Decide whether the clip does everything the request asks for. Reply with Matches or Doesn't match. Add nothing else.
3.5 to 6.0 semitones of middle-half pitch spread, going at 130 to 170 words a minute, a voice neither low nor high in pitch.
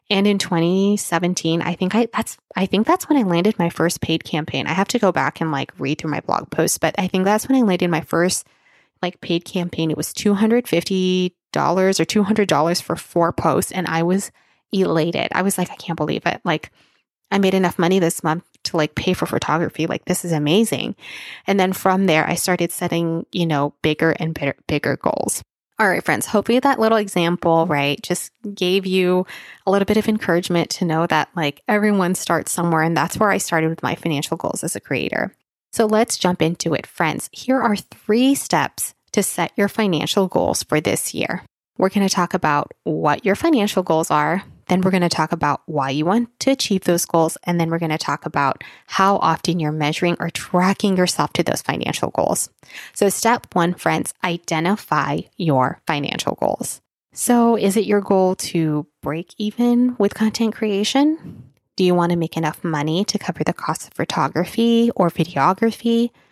Doesn't match